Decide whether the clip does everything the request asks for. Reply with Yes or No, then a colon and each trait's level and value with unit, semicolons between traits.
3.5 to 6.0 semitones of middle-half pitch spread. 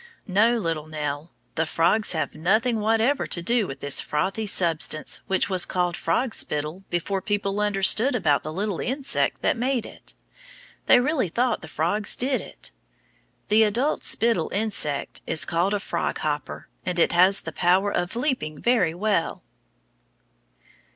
Yes: average, 5.2 semitones